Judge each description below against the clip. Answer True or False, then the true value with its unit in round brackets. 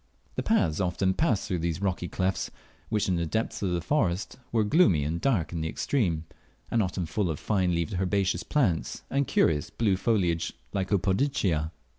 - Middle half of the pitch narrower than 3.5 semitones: False (3.9 semitones)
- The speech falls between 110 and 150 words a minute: False (175 wpm)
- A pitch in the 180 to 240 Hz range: False (95 Hz)